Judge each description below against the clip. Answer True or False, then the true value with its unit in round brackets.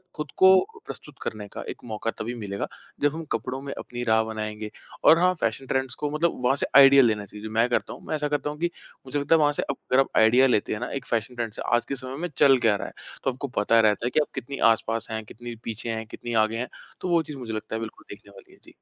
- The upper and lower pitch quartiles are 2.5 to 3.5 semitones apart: False (4.2 semitones)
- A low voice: True (120 Hz)